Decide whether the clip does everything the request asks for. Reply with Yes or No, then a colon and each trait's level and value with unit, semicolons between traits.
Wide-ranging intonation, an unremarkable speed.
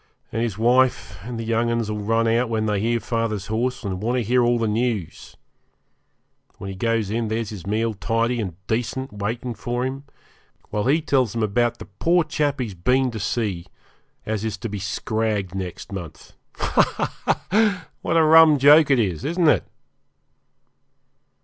No: average, 3.2 semitones; average, 180 wpm